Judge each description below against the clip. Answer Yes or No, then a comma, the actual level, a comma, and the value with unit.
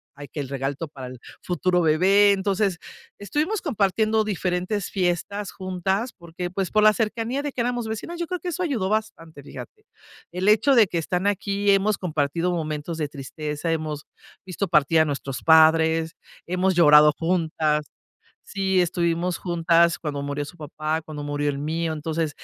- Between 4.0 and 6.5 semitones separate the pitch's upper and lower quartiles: Yes, average, 4.6 semitones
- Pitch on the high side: No, medium, 175 Hz